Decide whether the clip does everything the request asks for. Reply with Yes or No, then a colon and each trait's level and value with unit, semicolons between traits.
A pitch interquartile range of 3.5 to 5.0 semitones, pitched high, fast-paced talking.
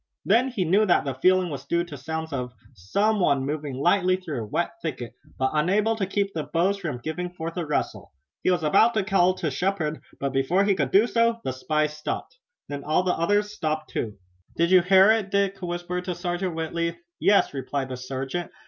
No: average, 4.7 semitones; medium, 175 Hz; fast, 210 wpm